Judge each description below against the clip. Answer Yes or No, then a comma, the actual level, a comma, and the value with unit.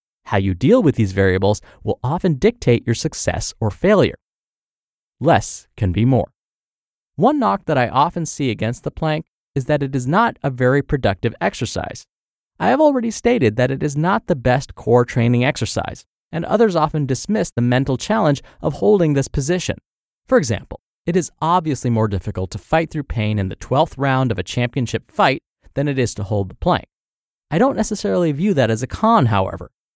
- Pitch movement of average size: No, wide, 6.5 semitones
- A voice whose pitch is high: No, low, 130 Hz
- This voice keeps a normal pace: Yes, average, 190 wpm